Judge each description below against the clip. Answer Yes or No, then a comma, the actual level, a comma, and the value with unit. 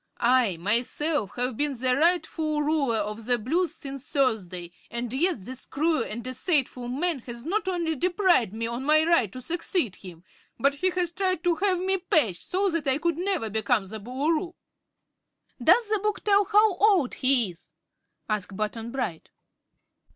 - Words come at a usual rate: Yes, average, 170 wpm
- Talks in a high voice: Yes, very high, 275 Hz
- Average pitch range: No, wide, 7.1 semitones